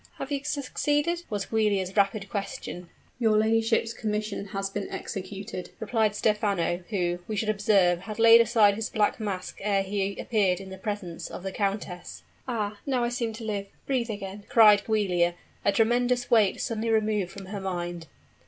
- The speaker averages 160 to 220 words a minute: Yes, average, 170 wpm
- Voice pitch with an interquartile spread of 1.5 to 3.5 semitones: Yes, narrow, 2.5 semitones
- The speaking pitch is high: Yes, high, 210 Hz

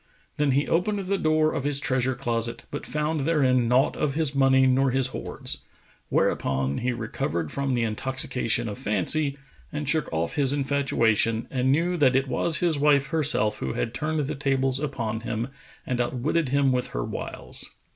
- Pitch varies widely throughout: No, average, 3.6 semitones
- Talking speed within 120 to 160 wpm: No, average, 175 wpm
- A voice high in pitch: No, low, 135 Hz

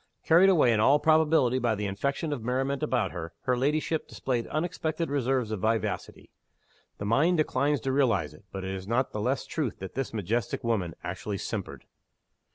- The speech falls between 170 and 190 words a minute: Yes, average, 180 wpm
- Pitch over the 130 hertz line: No, low, 125 Hz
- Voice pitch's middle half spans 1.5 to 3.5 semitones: No, wide, 5.4 semitones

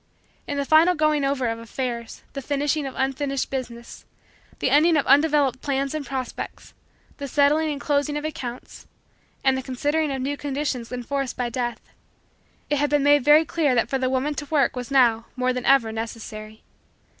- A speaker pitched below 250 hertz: No, very high, 275 Hz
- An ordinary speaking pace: Yes, average, 180 wpm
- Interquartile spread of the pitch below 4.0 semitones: Yes, narrow, 2.6 semitones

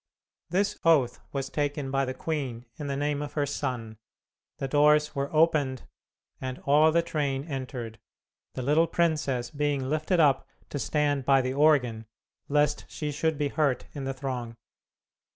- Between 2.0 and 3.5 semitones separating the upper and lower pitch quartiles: Yes, narrow, 2.4 semitones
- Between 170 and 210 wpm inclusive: No, average, 160 wpm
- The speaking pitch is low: No, medium, 145 Hz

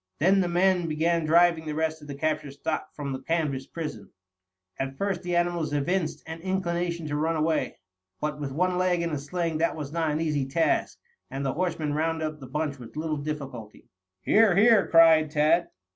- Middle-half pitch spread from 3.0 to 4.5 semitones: No, narrow, 2.6 semitones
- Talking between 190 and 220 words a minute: Yes, average, 195 wpm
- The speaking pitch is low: No, medium, 160 Hz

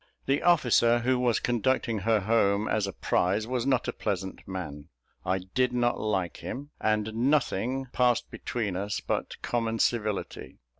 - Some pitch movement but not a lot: Yes, average, 3.8 semitones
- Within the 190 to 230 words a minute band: No, average, 155 wpm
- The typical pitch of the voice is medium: No, low, 115 Hz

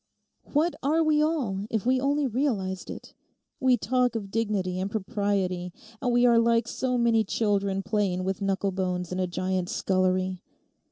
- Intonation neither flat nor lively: Yes, average, 4.8 semitones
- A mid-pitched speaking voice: No, high, 205 Hz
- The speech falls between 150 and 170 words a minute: Yes, average, 160 wpm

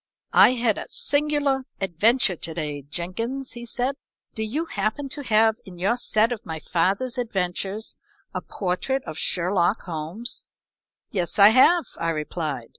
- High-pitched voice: Yes, high, 215 Hz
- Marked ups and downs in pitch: Yes, wide, 6.2 semitones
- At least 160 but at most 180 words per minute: No, average, 150 wpm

